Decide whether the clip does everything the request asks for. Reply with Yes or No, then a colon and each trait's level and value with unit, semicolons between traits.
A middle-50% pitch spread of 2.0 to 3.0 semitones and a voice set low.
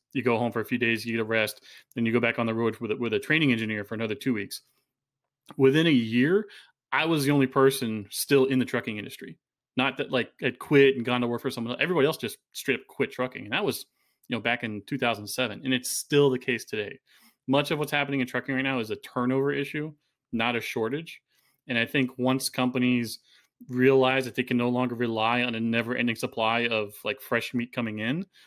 Yes: narrow, 2.5 semitones; low, 125 Hz